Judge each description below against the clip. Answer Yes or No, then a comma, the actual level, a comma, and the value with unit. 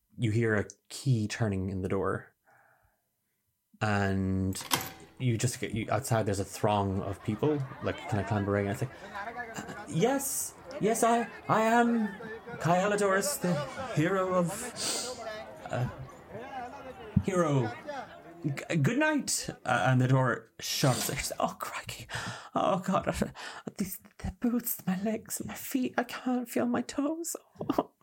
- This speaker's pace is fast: No, slow, 135 wpm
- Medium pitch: Yes, medium, 150 Hz